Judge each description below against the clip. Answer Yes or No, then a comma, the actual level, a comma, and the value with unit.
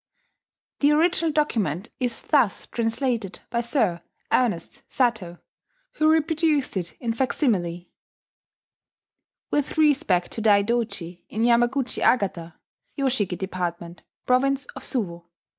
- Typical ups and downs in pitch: No, wide, 6.9 semitones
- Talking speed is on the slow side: Yes, slow, 105 wpm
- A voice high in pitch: Yes, high, 235 Hz